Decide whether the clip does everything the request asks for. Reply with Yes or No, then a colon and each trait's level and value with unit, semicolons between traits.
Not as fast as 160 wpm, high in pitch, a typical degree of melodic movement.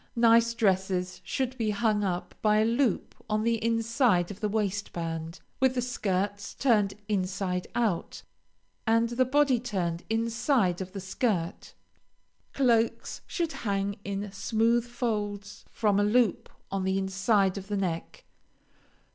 Yes: average, 140 wpm; high, 210 Hz; average, 3.3 semitones